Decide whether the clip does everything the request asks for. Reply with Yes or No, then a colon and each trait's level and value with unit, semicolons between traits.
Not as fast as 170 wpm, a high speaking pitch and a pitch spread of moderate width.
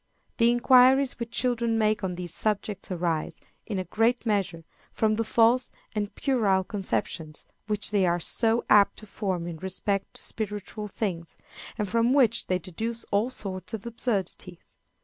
Yes: average, 160 wpm; high, 210 Hz; average, 3.7 semitones